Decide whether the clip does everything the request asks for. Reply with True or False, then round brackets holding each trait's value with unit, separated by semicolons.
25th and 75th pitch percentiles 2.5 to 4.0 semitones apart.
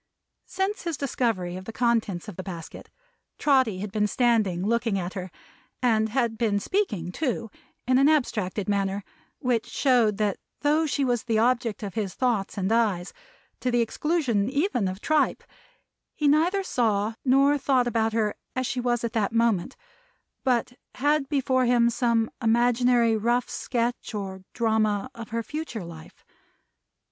True (3.6 semitones)